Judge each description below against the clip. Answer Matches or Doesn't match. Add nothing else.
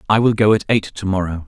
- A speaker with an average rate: Doesn't match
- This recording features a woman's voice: Doesn't match